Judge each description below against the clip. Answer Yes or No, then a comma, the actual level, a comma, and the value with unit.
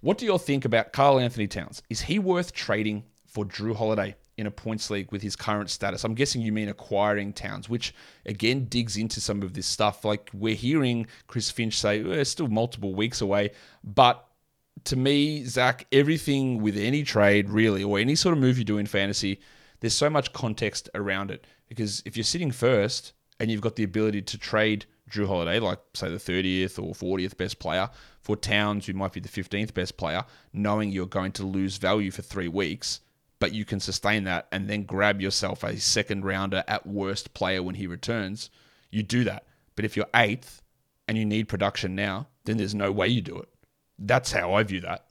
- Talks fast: Yes, fast, 210 wpm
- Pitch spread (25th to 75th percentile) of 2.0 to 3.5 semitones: Yes, average, 2.8 semitones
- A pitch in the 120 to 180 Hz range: No, low, 105 Hz